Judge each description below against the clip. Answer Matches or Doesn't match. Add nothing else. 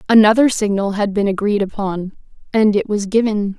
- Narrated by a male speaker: Doesn't match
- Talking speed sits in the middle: Matches